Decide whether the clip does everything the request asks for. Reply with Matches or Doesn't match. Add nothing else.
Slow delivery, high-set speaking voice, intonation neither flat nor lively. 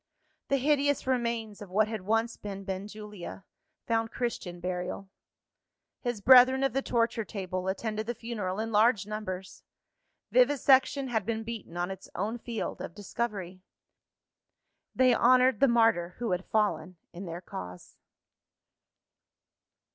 Matches